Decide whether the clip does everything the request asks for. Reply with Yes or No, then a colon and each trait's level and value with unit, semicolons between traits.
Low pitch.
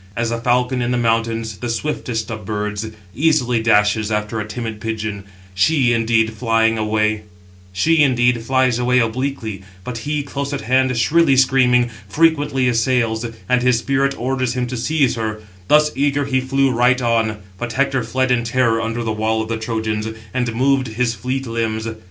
Yes: low, 120 Hz